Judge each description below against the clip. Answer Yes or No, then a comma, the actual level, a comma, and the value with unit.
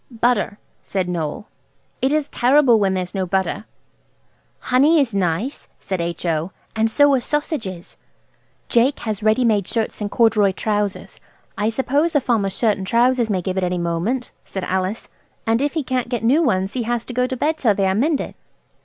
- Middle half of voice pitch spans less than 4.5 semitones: No, average, 5.0 semitones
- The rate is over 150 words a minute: Yes, average, 190 wpm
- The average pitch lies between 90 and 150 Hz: No, high, 220 Hz